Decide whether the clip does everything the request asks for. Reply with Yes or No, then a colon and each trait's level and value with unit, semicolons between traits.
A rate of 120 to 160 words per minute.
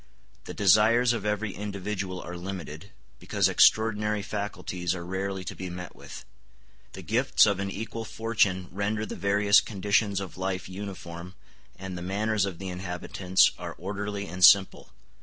Yes: average, 155 wpm